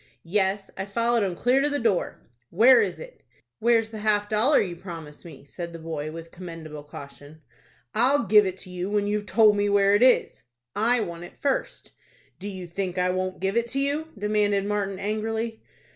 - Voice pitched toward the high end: Yes, high, 205 Hz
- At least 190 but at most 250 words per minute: Yes, average, 195 wpm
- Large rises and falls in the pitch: No, average, 3.9 semitones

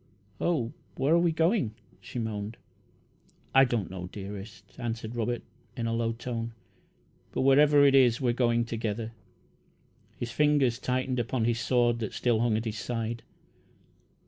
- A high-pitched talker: No, low, 120 Hz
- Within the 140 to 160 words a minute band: Yes, average, 150 wpm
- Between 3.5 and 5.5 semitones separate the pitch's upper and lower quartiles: No, narrow, 2.5 semitones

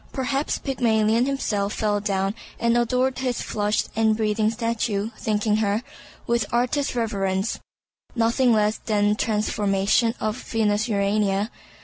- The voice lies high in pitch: Yes, high, 220 Hz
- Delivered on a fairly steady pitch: Yes, narrow, 2.3 semitones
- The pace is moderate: No, slow, 125 wpm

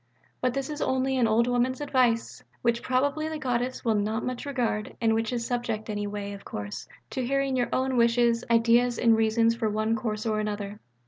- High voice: Yes, high, 235 Hz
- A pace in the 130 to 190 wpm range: No, average, 200 wpm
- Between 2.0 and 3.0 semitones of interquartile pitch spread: Yes, narrow, 2.6 semitones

